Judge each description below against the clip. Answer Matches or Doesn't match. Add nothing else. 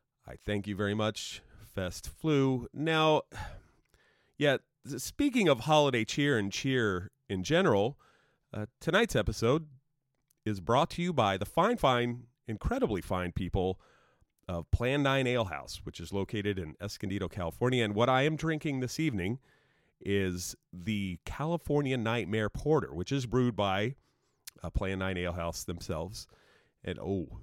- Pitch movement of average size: Doesn't match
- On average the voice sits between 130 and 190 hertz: Doesn't match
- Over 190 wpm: Doesn't match